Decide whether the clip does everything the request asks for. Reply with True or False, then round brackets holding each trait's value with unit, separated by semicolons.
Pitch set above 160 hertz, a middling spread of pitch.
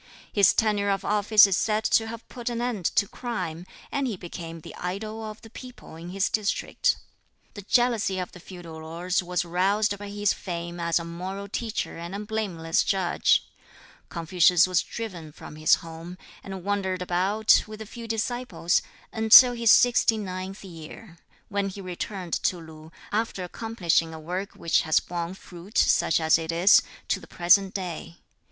True (190 Hz; 3.9 semitones)